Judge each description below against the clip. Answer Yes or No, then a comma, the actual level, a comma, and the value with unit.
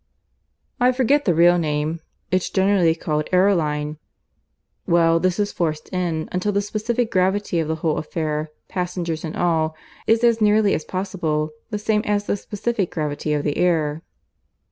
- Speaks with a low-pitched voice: No, medium, 175 Hz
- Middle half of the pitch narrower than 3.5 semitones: No, average, 4.5 semitones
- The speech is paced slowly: No, average, 160 wpm